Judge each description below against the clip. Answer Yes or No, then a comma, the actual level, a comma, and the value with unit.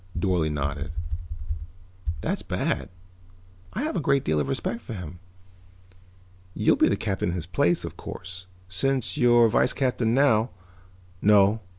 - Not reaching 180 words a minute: Yes, average, 150 wpm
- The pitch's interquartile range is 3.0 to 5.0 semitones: No, wide, 5.4 semitones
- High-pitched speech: No, very low, 95 Hz